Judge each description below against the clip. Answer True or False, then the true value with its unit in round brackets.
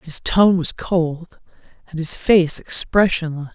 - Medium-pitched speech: True (170 Hz)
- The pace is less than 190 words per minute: True (135 wpm)